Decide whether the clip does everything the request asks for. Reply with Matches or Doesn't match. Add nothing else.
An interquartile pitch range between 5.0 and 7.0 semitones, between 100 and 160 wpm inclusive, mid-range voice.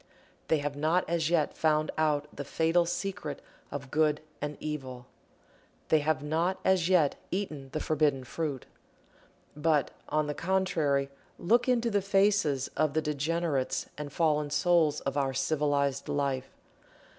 Doesn't match